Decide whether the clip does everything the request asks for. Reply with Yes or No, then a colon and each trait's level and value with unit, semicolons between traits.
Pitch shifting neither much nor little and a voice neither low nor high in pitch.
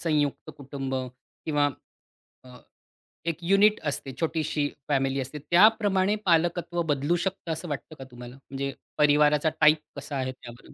Yes: average, 3.9 semitones; medium, 150 Hz